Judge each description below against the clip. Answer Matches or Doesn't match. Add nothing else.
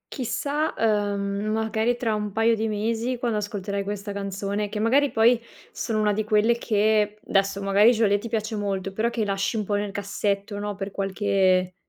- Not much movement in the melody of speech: Matches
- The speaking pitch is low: Doesn't match